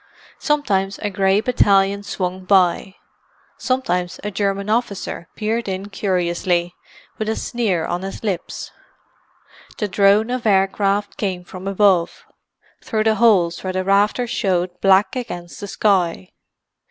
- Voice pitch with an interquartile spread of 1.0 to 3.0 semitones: Yes, narrow, 2.4 semitones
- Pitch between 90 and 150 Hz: No, high, 195 Hz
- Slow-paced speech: Yes, slow, 130 wpm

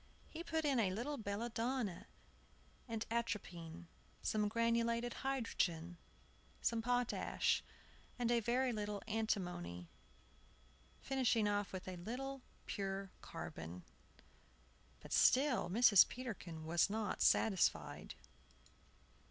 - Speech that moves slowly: Yes, slow, 100 wpm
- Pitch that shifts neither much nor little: Yes, average, 4.6 semitones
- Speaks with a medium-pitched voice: No, high, 220 Hz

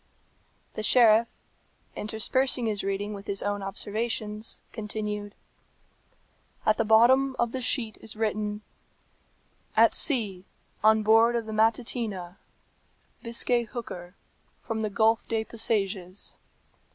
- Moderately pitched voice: No, high, 220 Hz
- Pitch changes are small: Yes, narrow, 2.0 semitones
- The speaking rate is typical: No, slow, 115 wpm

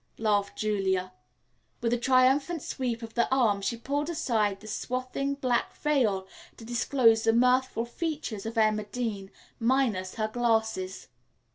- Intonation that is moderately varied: Yes, average, 3.2 semitones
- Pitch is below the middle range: No, high, 230 Hz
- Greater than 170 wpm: No, average, 140 wpm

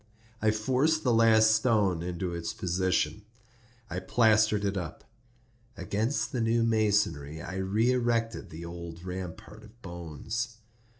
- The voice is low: Yes, low, 105 Hz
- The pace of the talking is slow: Yes, slow, 130 wpm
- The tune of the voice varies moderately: Yes, average, 4.4 semitones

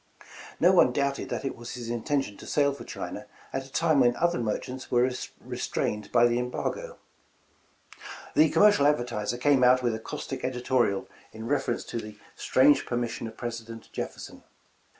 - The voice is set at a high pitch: No, low, 125 Hz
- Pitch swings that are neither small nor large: Yes, average, 3.0 semitones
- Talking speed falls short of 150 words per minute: No, average, 165 wpm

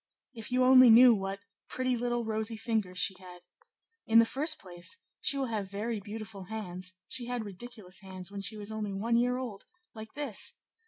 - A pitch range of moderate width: Yes, average, 3.6 semitones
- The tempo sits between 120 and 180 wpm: No, average, 190 wpm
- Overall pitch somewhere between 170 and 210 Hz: No, high, 220 Hz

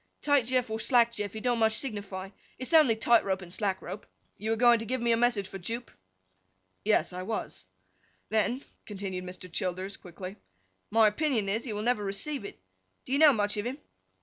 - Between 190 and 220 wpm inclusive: Yes, fast, 205 wpm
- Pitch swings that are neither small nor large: Yes, average, 3.5 semitones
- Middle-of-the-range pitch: No, high, 220 Hz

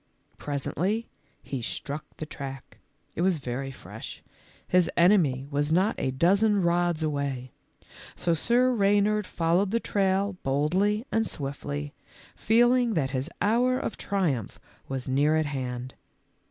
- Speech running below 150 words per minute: Yes, average, 140 wpm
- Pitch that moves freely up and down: Yes, wide, 6.5 semitones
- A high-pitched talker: No, medium, 165 Hz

